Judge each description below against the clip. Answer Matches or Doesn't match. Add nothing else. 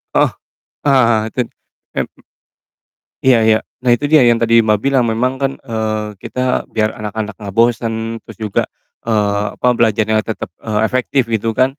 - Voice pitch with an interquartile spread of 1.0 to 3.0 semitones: Matches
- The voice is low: Matches